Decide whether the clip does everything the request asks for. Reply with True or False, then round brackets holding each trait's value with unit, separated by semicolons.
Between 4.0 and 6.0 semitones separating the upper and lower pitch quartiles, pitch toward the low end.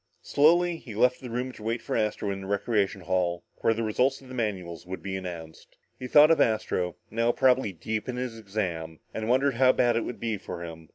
True (5.2 semitones; 110 Hz)